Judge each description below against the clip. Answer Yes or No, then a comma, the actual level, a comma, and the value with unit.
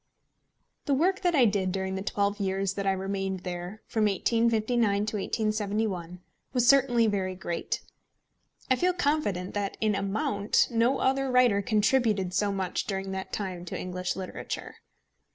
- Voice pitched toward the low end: No, high, 205 Hz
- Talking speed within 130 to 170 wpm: Yes, average, 150 wpm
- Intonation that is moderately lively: Yes, average, 3.5 semitones